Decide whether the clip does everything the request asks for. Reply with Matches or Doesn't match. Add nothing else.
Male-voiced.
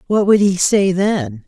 Doesn't match